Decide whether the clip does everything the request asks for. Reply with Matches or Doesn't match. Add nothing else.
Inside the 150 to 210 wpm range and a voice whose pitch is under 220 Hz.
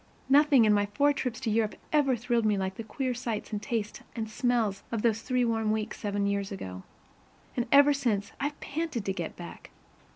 Doesn't match